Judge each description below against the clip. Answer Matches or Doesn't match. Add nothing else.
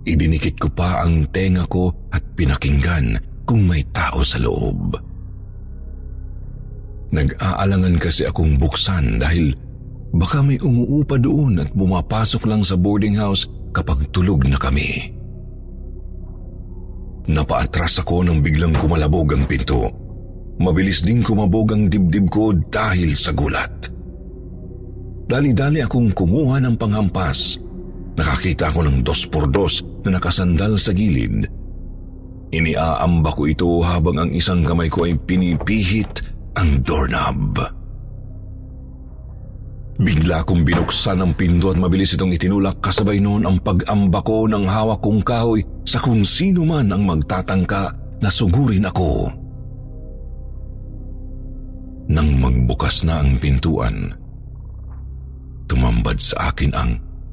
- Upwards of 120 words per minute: Doesn't match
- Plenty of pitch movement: Doesn't match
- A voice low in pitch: Matches